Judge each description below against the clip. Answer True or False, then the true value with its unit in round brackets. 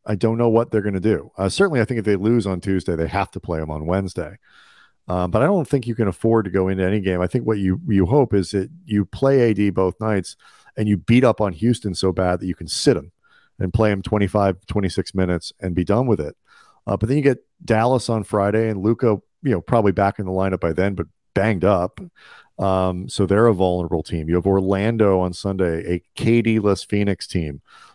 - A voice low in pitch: True (100 Hz)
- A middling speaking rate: False (240 wpm)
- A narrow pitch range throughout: False (3.1 semitones)